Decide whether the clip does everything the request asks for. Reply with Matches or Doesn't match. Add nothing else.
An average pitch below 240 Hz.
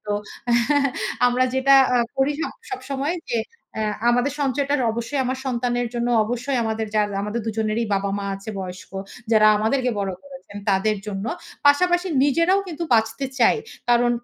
Doesn't match